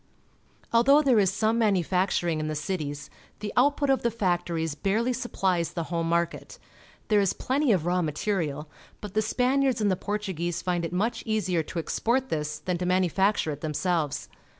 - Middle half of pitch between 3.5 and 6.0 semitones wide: Yes, average, 4.7 semitones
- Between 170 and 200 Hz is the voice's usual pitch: Yes, medium, 185 Hz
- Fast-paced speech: No, average, 175 wpm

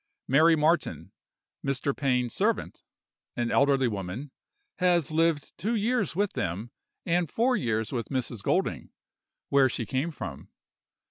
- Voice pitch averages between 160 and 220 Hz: No, medium, 140 Hz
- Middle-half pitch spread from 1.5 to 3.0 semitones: No, wide, 5.6 semitones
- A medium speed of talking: No, slow, 130 wpm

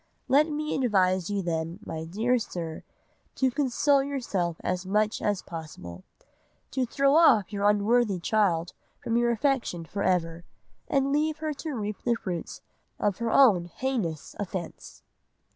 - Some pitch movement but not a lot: No, wide, 6.9 semitones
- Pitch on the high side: Yes, high, 210 Hz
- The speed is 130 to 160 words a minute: Yes, average, 145 wpm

